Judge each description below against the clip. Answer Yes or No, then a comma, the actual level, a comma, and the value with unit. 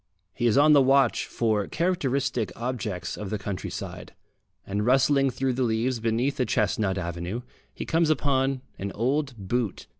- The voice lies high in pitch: No, low, 125 Hz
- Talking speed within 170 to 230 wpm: No, average, 155 wpm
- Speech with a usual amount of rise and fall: Yes, average, 4.4 semitones